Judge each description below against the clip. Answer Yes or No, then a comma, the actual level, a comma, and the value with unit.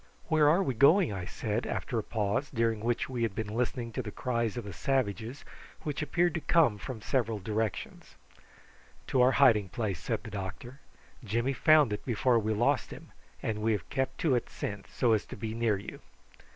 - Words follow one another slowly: No, average, 200 wpm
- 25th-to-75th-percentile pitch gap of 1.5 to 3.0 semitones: No, average, 3.8 semitones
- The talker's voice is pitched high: No, low, 115 Hz